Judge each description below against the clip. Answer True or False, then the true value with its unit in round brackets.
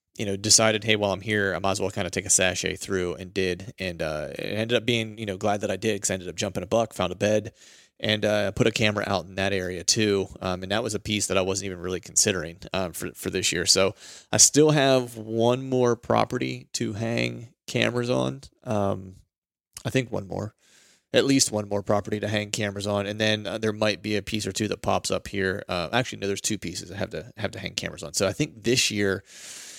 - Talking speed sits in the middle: False (255 wpm)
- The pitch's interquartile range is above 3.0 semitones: False (2.7 semitones)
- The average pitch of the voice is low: True (100 Hz)